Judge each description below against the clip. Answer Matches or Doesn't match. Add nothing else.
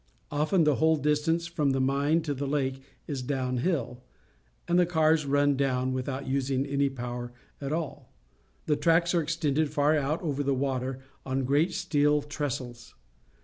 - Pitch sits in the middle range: Matches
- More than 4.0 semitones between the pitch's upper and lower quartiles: Doesn't match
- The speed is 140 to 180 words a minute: Matches